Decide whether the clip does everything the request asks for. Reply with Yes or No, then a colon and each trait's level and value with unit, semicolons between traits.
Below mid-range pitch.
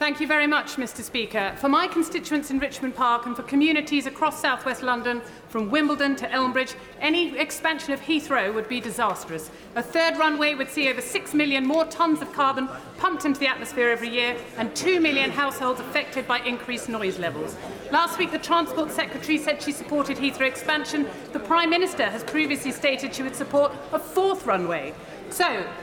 No: very high, 280 Hz